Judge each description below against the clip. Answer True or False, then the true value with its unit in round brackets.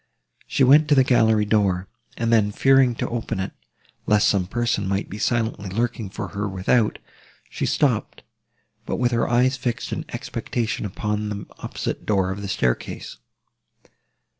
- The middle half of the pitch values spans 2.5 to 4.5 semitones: True (3.2 semitones)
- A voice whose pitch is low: True (105 Hz)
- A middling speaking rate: True (160 wpm)